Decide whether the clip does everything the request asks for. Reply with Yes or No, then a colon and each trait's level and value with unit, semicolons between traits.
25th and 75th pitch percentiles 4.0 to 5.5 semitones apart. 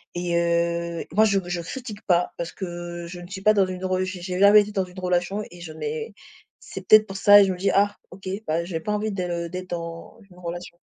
No: narrow, 2.5 semitones